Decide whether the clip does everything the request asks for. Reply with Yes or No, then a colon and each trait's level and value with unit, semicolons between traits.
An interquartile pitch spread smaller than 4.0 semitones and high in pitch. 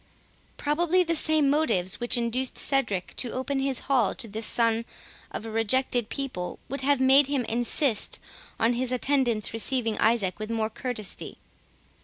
Yes: average, 3.5 semitones; high, 245 Hz